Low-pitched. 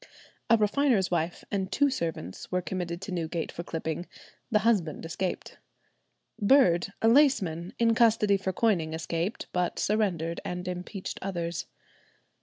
No: medium, 180 Hz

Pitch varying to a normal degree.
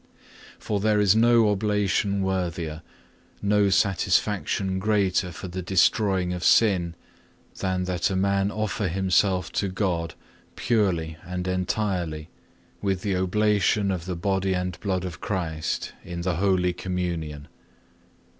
No: narrow, 2.1 semitones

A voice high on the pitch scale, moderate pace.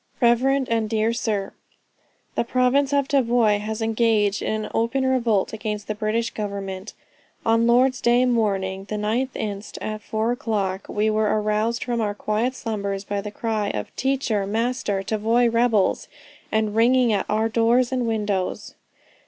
Yes: high, 220 Hz; average, 160 wpm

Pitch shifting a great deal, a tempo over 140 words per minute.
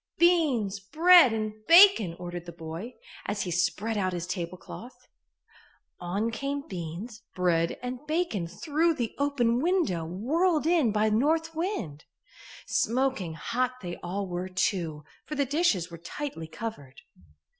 No: wide, 8.4 semitones; slow, 135 wpm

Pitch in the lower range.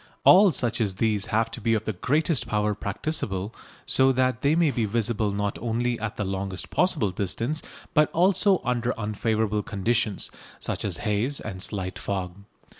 Yes: low, 110 Hz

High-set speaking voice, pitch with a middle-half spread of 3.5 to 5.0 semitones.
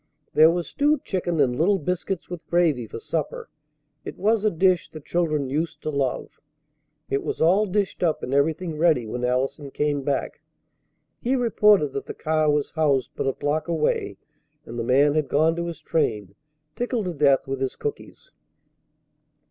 No: medium, 155 Hz; average, 4.2 semitones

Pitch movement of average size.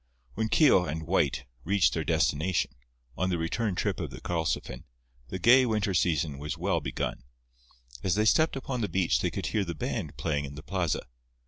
Yes: average, 4.5 semitones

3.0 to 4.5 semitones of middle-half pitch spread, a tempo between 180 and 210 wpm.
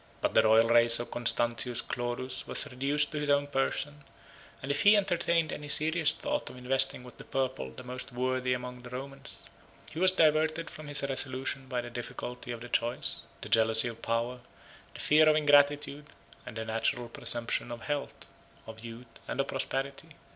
Yes: average, 3.5 semitones; average, 185 wpm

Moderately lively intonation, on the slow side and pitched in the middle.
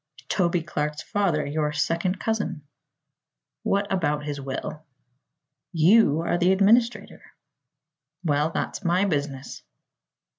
Yes: average, 4.3 semitones; slow, 105 wpm; medium, 165 Hz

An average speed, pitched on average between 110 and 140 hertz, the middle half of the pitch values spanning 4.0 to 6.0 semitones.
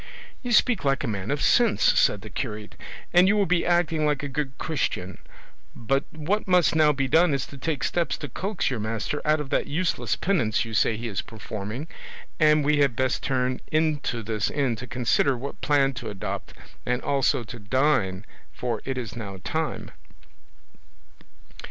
Yes: average, 180 wpm; low, 135 Hz; average, 5.2 semitones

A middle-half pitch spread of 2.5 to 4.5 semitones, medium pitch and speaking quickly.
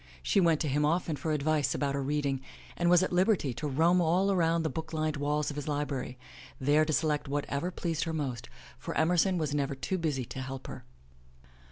Yes: average, 2.9 semitones; medium, 150 Hz; fast, 215 wpm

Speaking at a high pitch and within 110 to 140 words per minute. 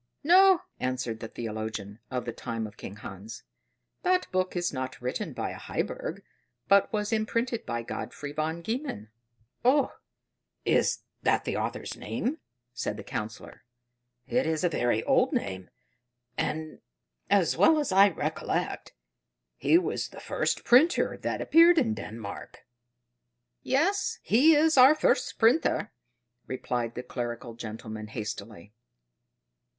No: medium, 145 Hz; slow, 135 wpm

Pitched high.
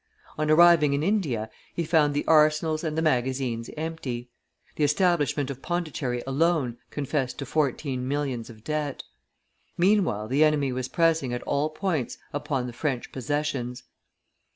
No: medium, 145 Hz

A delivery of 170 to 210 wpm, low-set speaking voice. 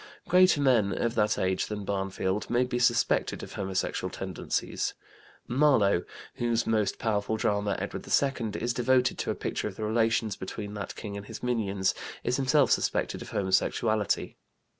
No: average, 160 wpm; low, 110 Hz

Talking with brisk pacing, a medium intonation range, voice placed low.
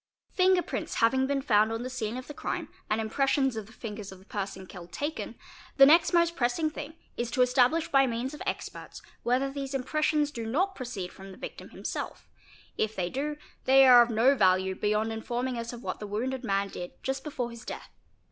No: fast, 215 wpm; average, 4.0 semitones; high, 245 Hz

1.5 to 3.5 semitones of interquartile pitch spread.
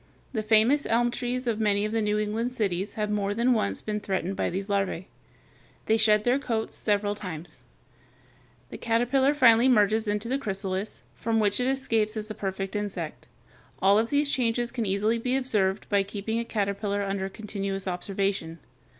Yes: average, 2.7 semitones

